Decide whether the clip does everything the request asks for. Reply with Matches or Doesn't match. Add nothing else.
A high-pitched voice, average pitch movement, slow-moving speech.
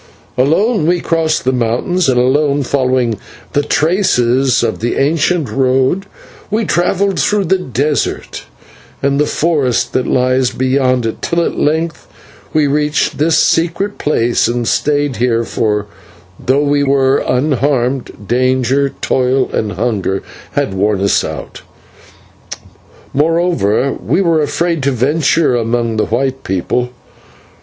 Doesn't match